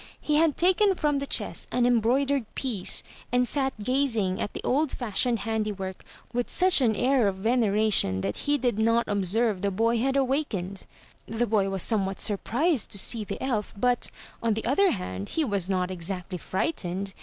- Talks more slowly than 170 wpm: No, average, 180 wpm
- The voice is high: Yes, high, 225 Hz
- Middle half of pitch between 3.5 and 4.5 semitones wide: No, average, 5.2 semitones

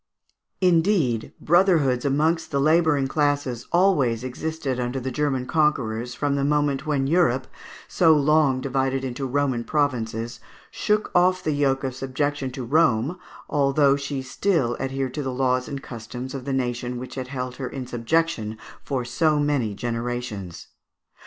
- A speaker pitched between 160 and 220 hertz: No, low, 135 Hz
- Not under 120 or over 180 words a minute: Yes, average, 150 wpm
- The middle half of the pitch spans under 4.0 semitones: Yes, average, 3.1 semitones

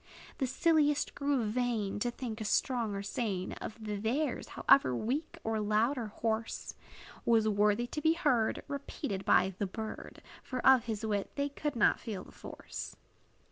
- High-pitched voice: Yes, high, 225 Hz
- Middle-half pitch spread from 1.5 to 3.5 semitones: No, average, 4.1 semitones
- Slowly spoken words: No, average, 165 wpm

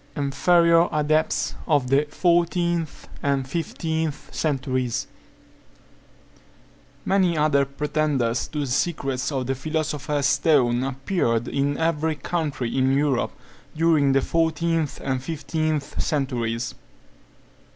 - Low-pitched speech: No, medium, 145 Hz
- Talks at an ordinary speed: No, slow, 100 wpm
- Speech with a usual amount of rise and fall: Yes, average, 3.2 semitones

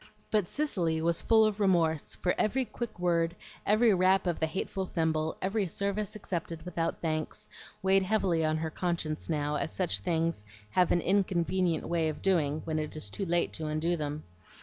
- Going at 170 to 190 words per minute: Yes, average, 180 wpm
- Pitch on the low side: No, medium, 170 Hz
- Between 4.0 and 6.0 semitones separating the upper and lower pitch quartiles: No, average, 3.3 semitones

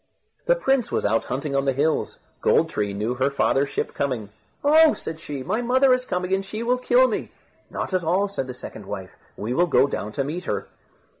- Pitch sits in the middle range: Yes, medium, 160 Hz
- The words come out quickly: Yes, fast, 220 wpm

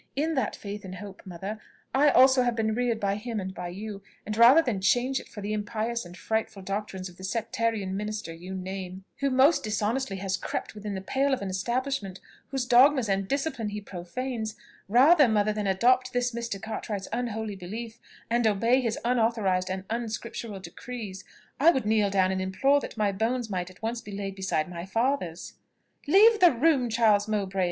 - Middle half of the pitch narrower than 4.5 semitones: Yes, average, 4.1 semitones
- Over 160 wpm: Yes, average, 190 wpm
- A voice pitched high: Yes, high, 215 Hz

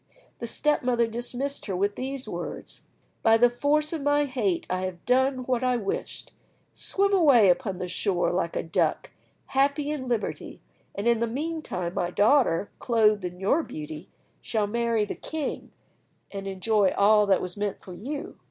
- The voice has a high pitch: Yes, high, 230 Hz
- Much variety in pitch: Yes, wide, 5.8 semitones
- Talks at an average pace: Yes, average, 170 wpm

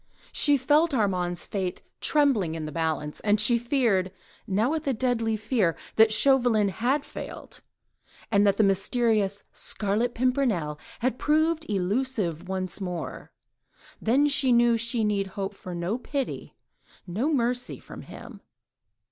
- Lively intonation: No, average, 5.0 semitones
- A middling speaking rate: No, slow, 130 wpm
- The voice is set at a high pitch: Yes, high, 220 Hz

